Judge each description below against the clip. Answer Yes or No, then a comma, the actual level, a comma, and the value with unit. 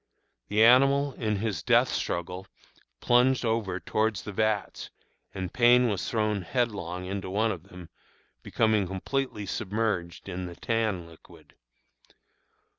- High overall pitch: No, low, 105 Hz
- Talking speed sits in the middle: No, slow, 125 wpm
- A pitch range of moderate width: Yes, average, 3.6 semitones